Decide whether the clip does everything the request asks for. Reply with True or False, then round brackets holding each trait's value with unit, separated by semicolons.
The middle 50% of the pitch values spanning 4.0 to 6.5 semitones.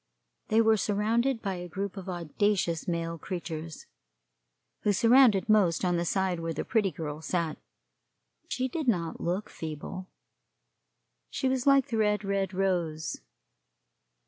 True (4.3 semitones)